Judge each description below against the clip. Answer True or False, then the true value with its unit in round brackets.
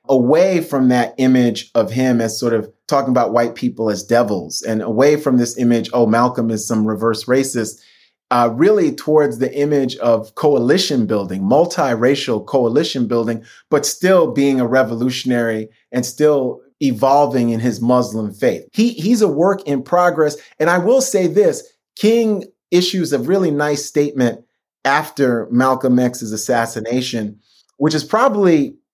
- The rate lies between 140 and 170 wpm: True (150 wpm)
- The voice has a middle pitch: False (130 Hz)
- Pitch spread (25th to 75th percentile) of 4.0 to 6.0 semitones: True (4.6 semitones)